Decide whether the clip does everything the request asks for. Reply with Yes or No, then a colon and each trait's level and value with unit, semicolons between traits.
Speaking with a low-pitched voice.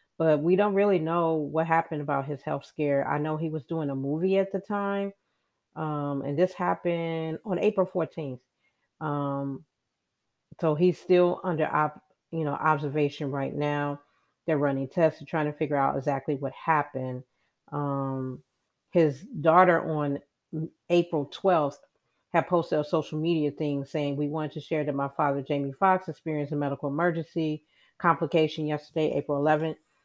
No: medium, 155 Hz